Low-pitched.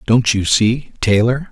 Yes: low, 115 Hz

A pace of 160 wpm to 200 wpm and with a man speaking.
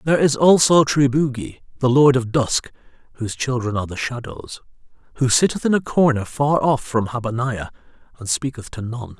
Yes: average, 170 wpm; male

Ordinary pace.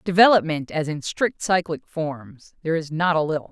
Yes: average, 190 wpm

